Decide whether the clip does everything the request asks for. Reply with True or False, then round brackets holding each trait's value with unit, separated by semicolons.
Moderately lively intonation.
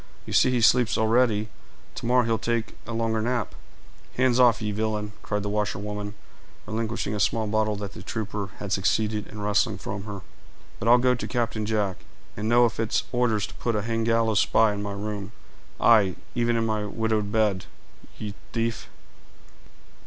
False (1.9 semitones)